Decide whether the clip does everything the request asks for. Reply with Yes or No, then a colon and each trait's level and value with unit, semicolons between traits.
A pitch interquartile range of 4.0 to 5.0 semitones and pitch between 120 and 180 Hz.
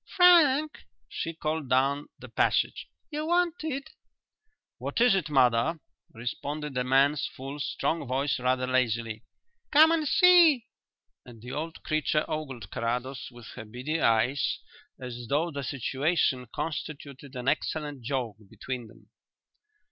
Yes: average, 4.6 semitones; medium, 140 Hz